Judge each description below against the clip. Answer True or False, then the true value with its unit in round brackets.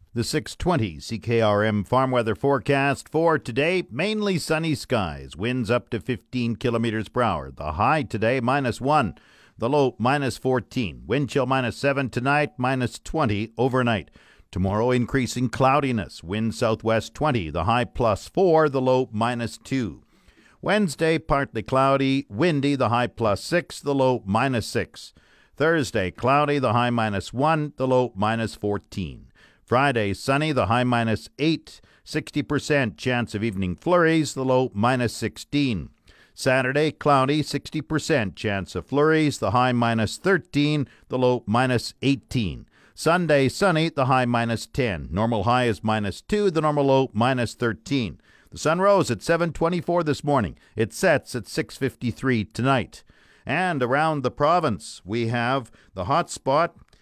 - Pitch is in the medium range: False (125 Hz)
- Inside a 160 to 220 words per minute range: False (145 wpm)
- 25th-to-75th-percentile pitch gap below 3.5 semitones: False (4.3 semitones)